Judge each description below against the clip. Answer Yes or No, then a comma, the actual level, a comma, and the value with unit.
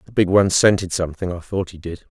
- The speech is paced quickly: Yes, fast, 250 wpm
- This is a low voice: Yes, very low, 90 Hz